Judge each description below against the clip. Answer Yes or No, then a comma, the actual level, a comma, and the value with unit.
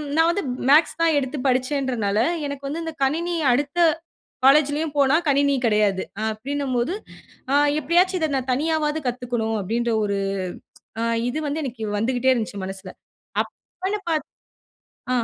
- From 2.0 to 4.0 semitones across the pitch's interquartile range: No, average, 4.7 semitones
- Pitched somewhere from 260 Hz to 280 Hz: Yes, very high, 275 Hz